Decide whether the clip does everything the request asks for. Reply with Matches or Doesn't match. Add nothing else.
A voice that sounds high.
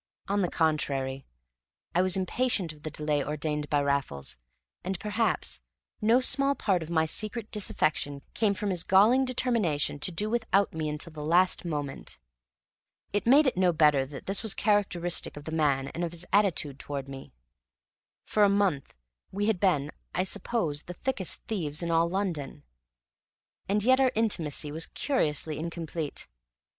Doesn't match